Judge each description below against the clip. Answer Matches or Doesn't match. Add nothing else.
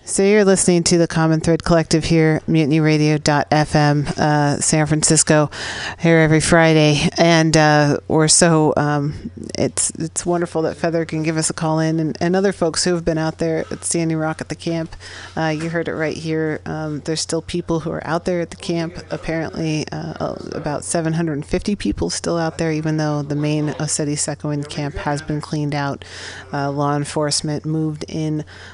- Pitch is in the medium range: Matches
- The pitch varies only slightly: Matches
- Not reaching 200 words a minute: Matches